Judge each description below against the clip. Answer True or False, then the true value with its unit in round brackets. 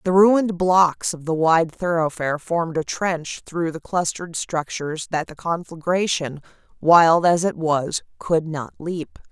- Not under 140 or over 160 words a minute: True (155 wpm)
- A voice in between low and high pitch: True (165 Hz)